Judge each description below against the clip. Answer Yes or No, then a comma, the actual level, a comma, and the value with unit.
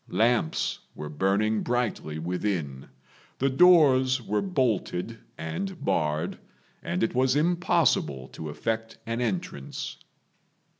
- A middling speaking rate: No, slow, 105 wpm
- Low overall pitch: Yes, low, 110 Hz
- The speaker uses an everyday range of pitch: No, wide, 8.2 semitones